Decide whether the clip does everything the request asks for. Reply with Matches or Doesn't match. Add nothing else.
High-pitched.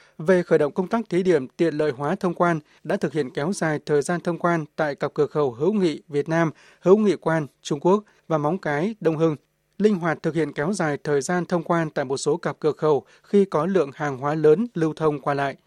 Doesn't match